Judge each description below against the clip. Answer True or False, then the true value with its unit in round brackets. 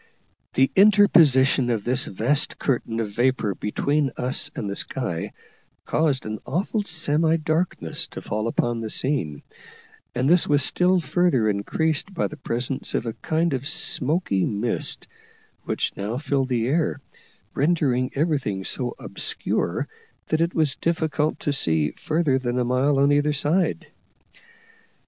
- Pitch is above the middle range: False (135 Hz)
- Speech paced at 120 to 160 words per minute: True (145 wpm)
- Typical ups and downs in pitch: True (4.8 semitones)